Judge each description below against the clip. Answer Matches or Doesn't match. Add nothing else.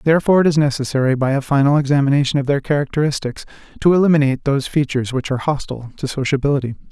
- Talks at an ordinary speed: Matches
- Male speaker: Matches